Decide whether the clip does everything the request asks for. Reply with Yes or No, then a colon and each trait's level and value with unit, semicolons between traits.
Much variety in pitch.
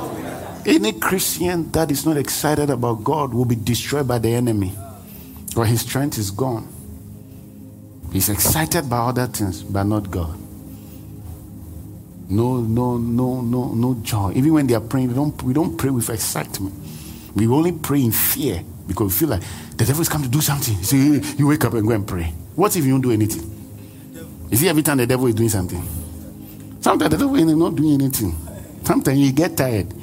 Yes: wide, 5.7 semitones